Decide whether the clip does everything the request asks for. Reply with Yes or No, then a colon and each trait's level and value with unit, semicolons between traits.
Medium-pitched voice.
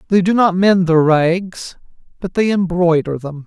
Yes: medium, 175 Hz